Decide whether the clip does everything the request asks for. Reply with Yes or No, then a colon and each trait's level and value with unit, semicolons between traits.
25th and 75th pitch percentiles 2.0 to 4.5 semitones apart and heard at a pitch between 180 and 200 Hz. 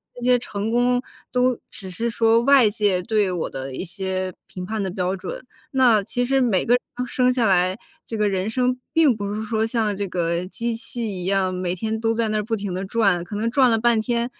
No: average, 4.0 semitones; high, 220 Hz